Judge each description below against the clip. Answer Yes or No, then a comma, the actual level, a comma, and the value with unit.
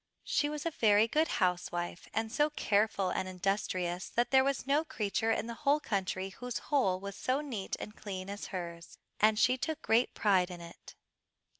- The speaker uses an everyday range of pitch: No, wide, 5.7 semitones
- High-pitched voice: Yes, high, 210 Hz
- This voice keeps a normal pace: Yes, average, 185 wpm